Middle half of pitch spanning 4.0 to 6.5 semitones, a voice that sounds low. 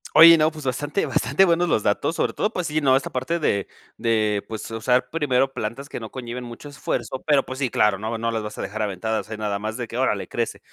Yes: average, 4.9 semitones; low, 125 Hz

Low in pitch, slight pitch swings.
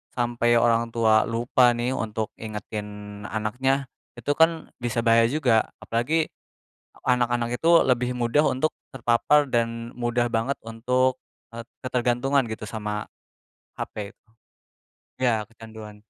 Yes: low, 120 Hz; narrow, 2.1 semitones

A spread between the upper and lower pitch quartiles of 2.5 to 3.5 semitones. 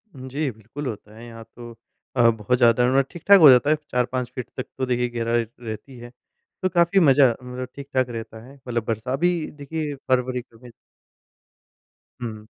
Yes: average, 2.8 semitones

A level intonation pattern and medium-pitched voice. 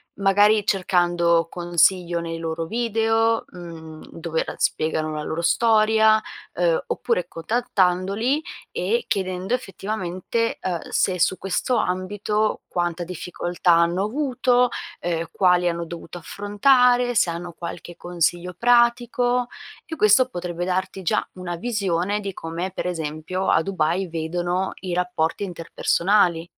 No: average, 4.0 semitones; medium, 180 Hz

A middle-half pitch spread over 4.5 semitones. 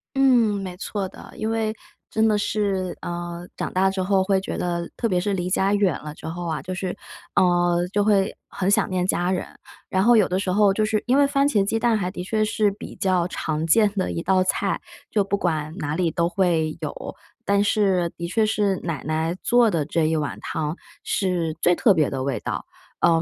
No: average, 3.2 semitones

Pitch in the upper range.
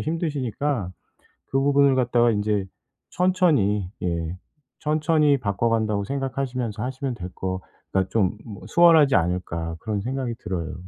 No: low, 120 Hz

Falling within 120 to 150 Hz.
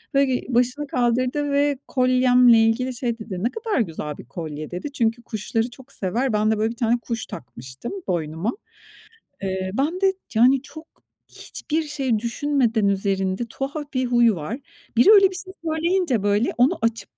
No: high, 240 Hz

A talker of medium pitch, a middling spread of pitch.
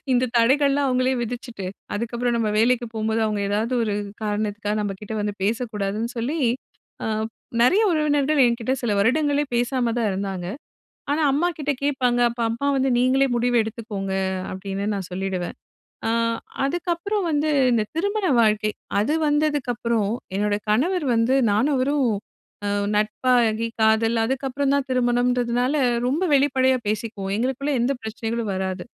No: high, 240 Hz; average, 4.2 semitones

